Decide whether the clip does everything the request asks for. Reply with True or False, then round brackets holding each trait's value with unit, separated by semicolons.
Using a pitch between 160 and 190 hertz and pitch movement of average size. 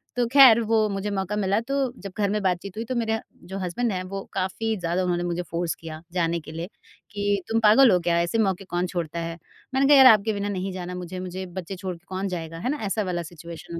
True (185 Hz; 3.2 semitones)